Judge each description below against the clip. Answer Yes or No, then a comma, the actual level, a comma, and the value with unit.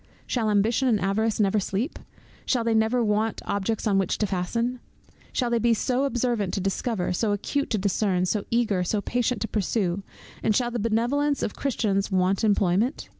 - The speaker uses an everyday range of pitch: Yes, average, 3.3 semitones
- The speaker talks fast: No, average, 180 wpm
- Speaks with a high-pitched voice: Yes, high, 220 Hz